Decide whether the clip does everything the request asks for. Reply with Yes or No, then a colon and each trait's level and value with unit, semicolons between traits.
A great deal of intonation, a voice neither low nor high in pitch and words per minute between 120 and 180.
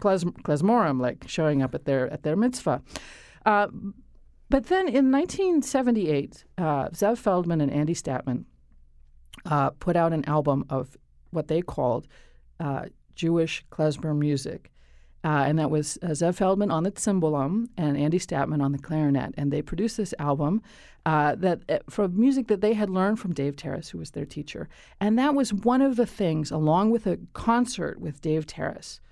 Yes: wide, 6.4 semitones; medium, 160 Hz; average, 175 wpm